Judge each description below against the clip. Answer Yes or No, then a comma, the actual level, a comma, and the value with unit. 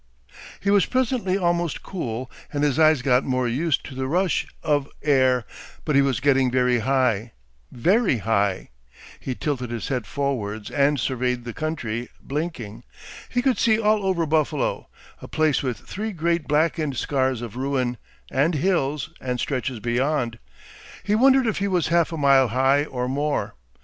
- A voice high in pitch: No, medium, 140 Hz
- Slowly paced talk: No, average, 165 wpm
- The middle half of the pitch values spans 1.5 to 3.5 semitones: No, average, 5.0 semitones